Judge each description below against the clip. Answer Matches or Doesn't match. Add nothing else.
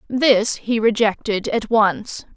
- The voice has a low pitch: Doesn't match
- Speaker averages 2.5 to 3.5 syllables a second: Matches